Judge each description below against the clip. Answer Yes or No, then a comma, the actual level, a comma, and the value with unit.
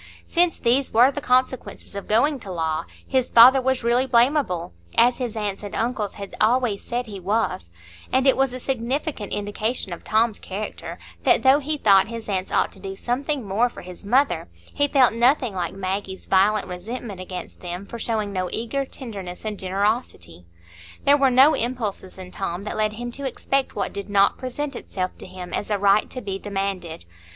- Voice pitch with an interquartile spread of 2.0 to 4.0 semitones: No, average, 4.7 semitones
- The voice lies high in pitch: Yes, high, 215 Hz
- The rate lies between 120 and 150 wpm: No, average, 190 wpm